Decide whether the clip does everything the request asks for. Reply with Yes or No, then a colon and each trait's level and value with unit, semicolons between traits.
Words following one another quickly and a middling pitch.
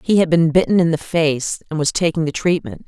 Yes: fast, 250 wpm; medium, 160 Hz